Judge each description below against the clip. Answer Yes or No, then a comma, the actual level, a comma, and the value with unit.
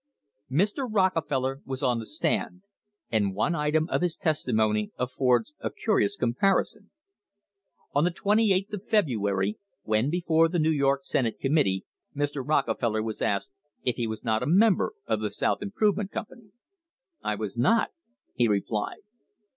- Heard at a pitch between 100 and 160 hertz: Yes, medium, 140 Hz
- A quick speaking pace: No, average, 155 wpm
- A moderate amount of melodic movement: No, wide, 8.7 semitones